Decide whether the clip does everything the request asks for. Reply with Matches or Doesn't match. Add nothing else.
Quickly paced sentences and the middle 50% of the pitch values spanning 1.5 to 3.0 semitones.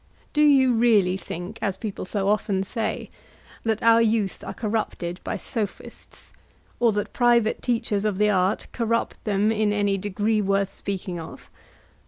Doesn't match